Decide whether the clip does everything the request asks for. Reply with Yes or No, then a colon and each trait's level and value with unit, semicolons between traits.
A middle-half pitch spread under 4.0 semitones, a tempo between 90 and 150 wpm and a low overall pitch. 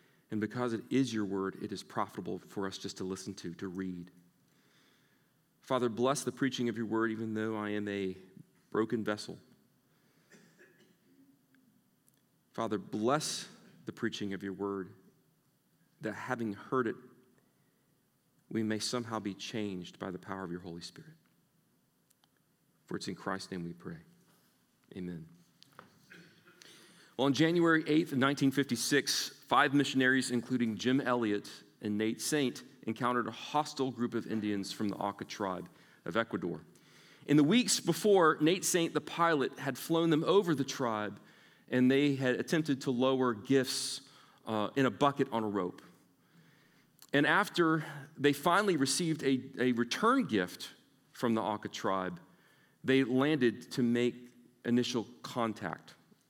No: average, 5.3 semitones; average, 145 wpm; low, 120 Hz